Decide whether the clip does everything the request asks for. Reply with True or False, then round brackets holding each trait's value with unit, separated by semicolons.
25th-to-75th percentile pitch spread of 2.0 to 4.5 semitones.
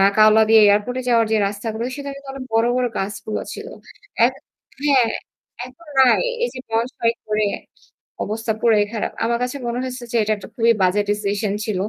True (2.8 semitones)